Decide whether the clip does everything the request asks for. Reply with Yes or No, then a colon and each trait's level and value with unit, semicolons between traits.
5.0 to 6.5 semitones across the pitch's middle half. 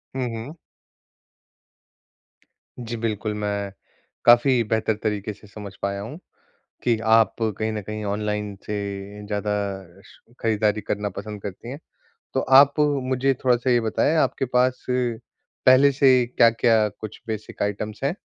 No: average, 3.2 semitones